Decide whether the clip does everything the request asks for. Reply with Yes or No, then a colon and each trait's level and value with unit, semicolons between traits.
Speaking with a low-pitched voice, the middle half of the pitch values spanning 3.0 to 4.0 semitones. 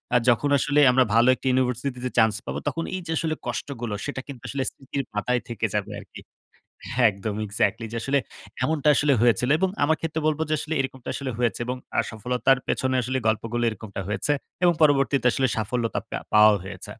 Yes: low, 125 Hz; average, 3.5 semitones